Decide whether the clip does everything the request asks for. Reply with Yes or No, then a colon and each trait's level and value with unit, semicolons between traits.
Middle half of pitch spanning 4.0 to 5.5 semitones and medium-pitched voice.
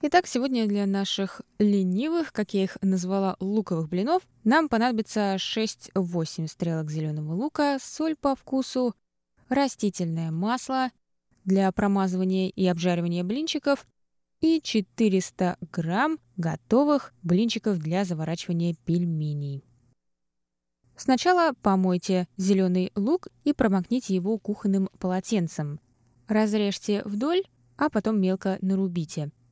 No: average, 5.0 semitones; high, 195 Hz